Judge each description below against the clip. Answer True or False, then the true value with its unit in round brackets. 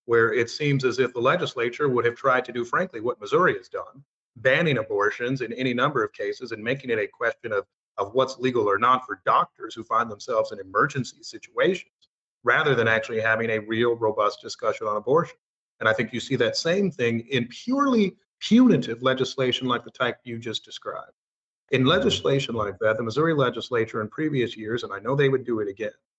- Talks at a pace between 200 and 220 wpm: True (205 wpm)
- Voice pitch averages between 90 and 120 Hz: False (130 Hz)